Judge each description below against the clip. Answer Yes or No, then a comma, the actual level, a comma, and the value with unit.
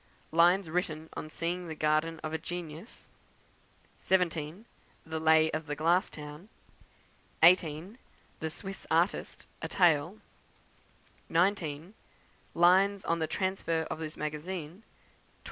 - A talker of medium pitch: Yes, medium, 165 Hz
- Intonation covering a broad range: No, average, 2.7 semitones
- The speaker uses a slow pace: Yes, slow, 120 wpm